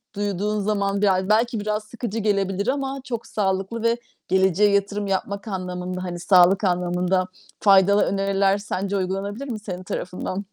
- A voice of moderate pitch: No, high, 200 Hz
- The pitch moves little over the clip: Yes, narrow, 2.0 semitones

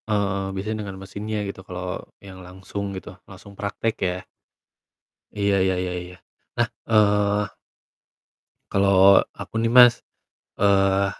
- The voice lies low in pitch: Yes, low, 100 Hz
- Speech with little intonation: Yes, narrow, 1.4 semitones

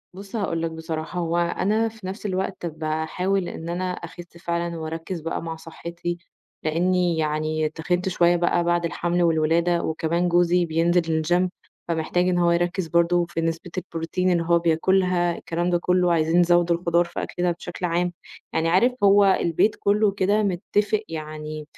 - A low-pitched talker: No, medium, 175 Hz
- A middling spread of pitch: No, narrow, 1.6 semitones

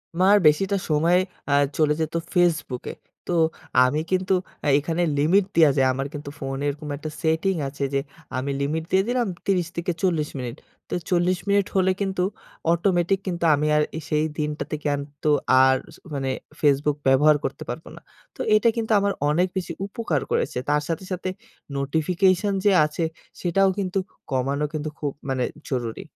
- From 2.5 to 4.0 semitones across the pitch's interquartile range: No, average, 4.4 semitones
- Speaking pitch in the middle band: Yes, medium, 160 Hz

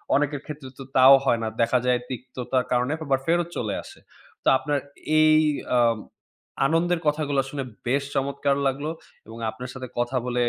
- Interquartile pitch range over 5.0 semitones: No, average, 2.7 semitones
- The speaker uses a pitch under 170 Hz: Yes, low, 135 Hz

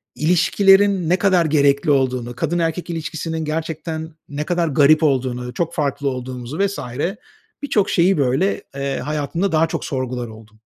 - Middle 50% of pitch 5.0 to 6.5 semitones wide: No, average, 4.3 semitones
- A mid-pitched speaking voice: Yes, medium, 155 Hz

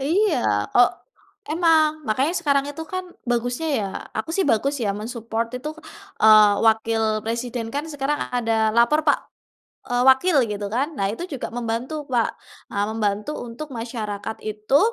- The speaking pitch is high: Yes, high, 245 Hz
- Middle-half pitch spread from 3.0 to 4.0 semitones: No, average, 4.6 semitones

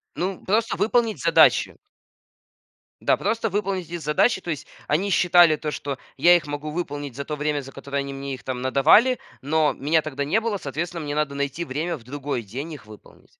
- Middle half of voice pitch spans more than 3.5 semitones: Yes, average, 4.0 semitones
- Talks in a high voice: No, medium, 150 Hz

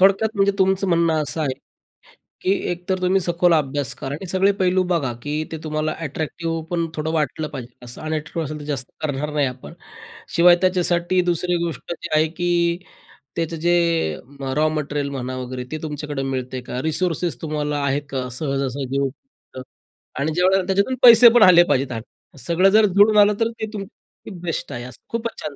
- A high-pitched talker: No, medium, 160 Hz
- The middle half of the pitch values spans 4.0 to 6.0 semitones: Yes, average, 4.4 semitones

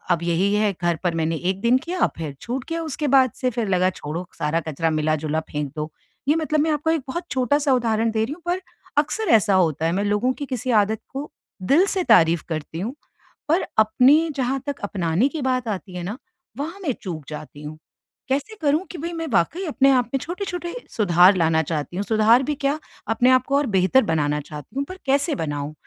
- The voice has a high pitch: Yes, high, 225 Hz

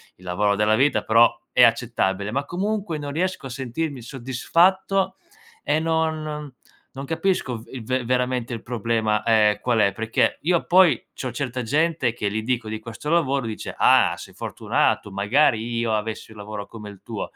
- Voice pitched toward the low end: Yes, low, 125 Hz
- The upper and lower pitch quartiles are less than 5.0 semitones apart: No, wide, 5.4 semitones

